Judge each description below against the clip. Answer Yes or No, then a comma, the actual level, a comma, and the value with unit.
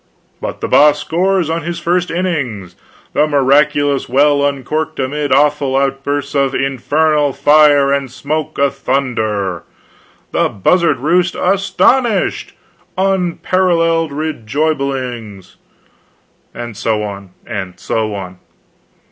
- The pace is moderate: No, slow, 105 wpm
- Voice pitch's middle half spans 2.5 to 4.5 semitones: Yes, average, 3.9 semitones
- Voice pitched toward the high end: No, medium, 140 Hz